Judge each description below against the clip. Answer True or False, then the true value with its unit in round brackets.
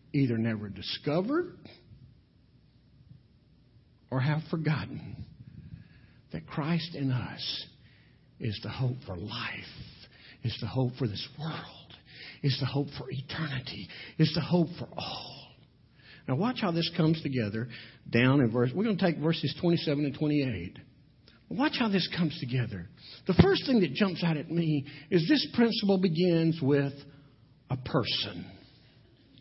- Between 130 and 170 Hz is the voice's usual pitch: True (140 Hz)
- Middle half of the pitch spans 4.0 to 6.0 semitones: True (5.4 semitones)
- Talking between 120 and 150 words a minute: True (140 wpm)